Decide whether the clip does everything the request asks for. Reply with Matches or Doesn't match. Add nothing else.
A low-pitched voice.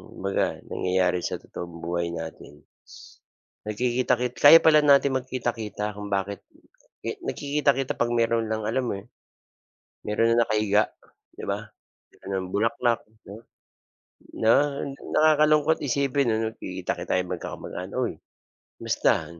Matches